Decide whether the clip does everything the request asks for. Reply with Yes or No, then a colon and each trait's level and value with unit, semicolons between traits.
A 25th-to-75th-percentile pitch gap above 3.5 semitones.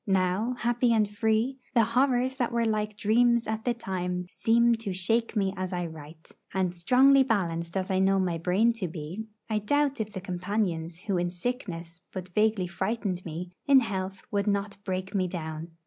Yes: average, 4.2 semitones